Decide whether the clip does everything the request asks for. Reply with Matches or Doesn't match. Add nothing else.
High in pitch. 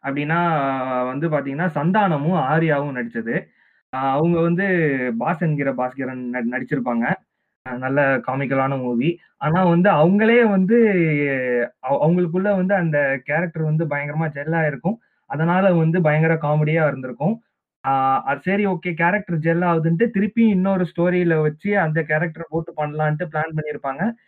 Doesn't match